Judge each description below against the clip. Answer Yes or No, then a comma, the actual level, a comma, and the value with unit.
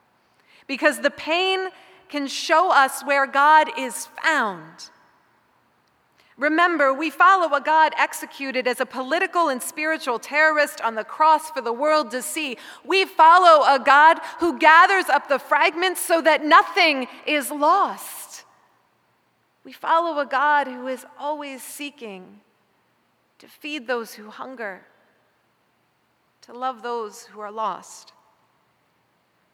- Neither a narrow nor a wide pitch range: Yes, average, 3.4 semitones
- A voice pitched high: Yes, very high, 295 Hz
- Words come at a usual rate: No, slow, 130 wpm